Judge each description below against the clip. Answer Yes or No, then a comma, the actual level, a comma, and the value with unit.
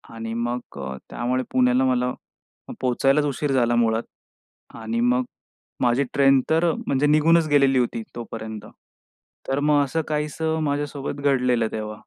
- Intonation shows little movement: No, average, 3.4 semitones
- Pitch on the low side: Yes, low, 130 Hz